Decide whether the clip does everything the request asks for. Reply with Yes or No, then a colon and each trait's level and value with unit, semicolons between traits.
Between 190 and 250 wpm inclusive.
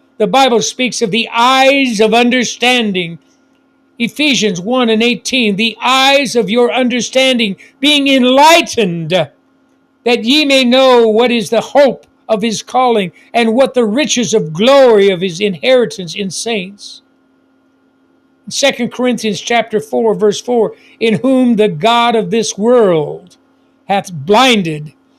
No: slow, 135 wpm